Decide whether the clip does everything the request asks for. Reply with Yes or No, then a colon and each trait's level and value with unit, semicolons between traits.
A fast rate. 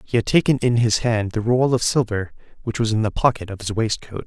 Yes: fast, 255 wpm